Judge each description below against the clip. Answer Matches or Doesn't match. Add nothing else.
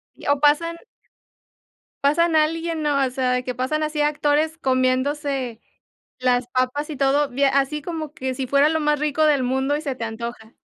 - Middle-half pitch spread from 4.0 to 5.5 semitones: Doesn't match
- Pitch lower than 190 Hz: Doesn't match